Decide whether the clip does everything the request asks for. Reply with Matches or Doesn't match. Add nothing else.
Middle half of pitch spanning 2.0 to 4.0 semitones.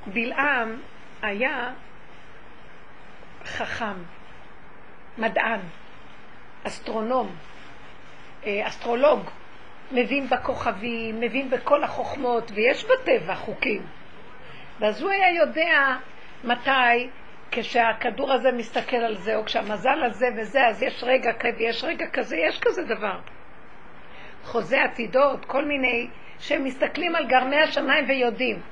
Matches